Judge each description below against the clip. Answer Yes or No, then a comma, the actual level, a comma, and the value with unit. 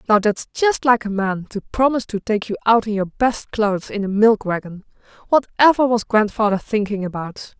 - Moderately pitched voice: No, high, 215 Hz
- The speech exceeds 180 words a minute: Yes, average, 195 wpm